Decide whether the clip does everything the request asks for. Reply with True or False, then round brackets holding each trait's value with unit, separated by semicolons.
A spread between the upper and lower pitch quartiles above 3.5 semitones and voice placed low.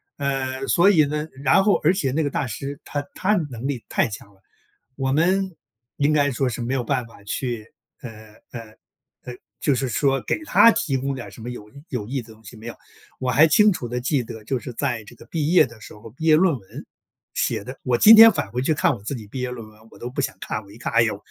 True (4.0 semitones; 130 Hz)